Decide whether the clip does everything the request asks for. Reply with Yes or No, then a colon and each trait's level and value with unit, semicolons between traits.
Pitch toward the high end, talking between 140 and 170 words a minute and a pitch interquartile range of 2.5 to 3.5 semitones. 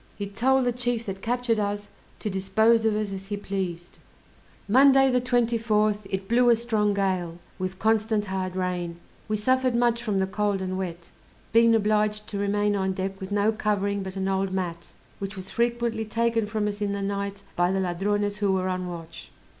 No: high, 205 Hz; average, 195 wpm; average, 2.8 semitones